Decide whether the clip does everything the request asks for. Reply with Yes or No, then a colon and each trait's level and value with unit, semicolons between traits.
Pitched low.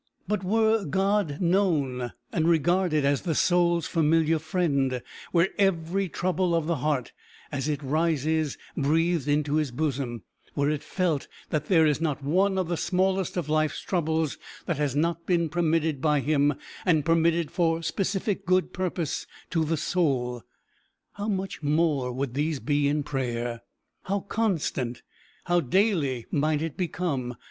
No: medium, 160 Hz